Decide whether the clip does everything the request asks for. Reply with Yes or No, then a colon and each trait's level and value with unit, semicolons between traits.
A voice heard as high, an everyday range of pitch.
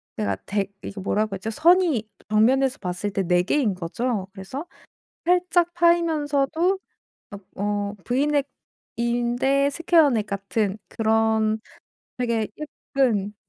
No: high, 230 Hz; wide, 5.9 semitones